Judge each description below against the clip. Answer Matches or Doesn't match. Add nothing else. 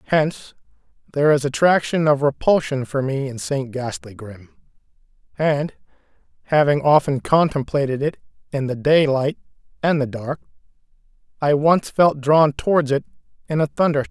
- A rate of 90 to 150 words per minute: Matches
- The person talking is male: Matches